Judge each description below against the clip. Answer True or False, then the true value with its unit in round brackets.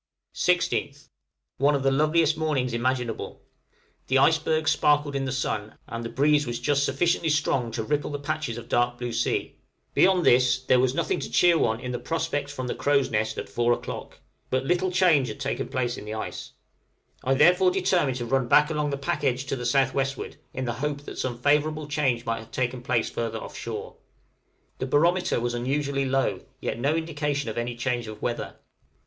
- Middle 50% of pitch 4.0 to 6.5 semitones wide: False (3.4 semitones)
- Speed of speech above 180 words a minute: True (200 wpm)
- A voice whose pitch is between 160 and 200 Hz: False (135 Hz)